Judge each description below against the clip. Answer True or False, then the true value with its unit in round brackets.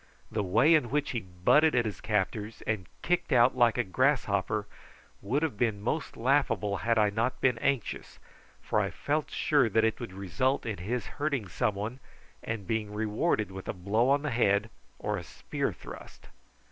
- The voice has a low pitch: True (115 Hz)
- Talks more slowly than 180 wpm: False (185 wpm)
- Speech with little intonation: False (4.2 semitones)